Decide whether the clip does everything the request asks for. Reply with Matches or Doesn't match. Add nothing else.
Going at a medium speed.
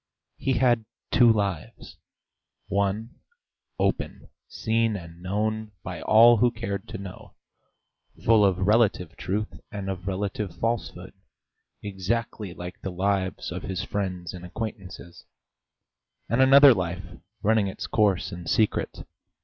Doesn't match